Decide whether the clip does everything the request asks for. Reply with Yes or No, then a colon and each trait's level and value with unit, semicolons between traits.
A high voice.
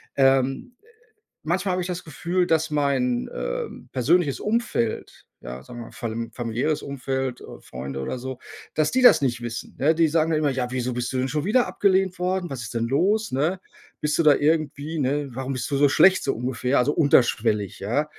No: medium, 140 Hz